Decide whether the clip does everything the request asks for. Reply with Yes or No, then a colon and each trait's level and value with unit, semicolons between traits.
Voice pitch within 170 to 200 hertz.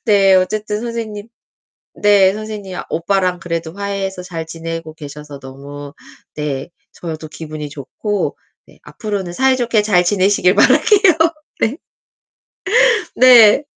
Yes: high, 190 Hz